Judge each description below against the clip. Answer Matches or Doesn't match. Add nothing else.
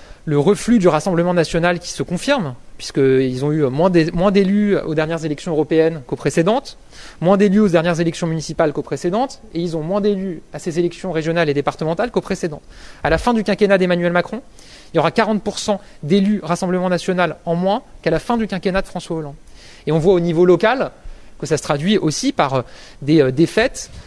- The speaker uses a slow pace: Doesn't match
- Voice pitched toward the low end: Doesn't match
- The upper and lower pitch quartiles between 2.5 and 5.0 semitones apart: Matches